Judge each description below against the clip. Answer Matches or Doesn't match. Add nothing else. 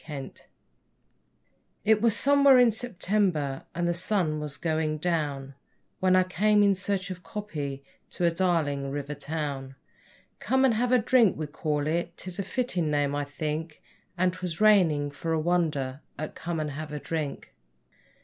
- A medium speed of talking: Matches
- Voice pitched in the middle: Matches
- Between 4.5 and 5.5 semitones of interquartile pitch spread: Matches